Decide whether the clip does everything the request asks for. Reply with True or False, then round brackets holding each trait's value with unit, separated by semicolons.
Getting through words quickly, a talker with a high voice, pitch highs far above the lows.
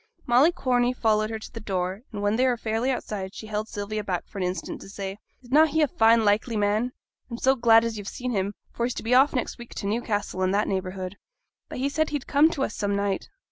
False (255 wpm; 220 Hz; 3.5 semitones)